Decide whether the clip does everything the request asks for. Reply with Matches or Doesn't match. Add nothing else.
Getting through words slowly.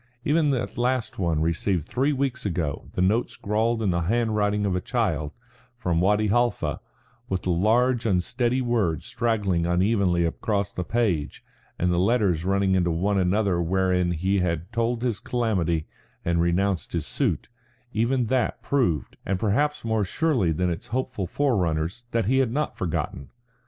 Doesn't match